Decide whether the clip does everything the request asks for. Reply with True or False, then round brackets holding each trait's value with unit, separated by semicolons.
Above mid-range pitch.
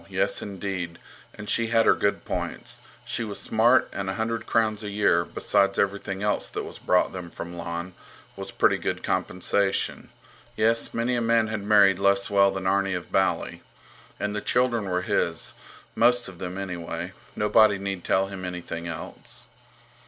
False (100 Hz)